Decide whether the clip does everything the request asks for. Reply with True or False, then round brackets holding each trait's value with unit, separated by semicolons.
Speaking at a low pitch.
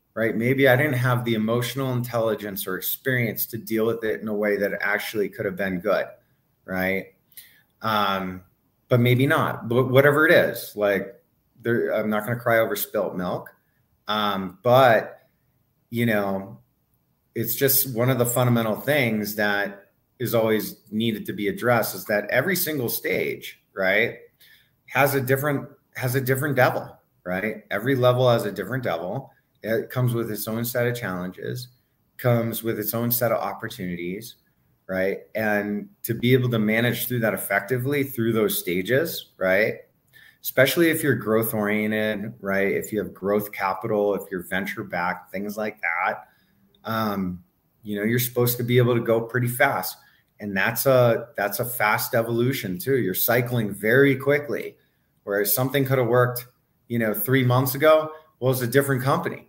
True (115 Hz)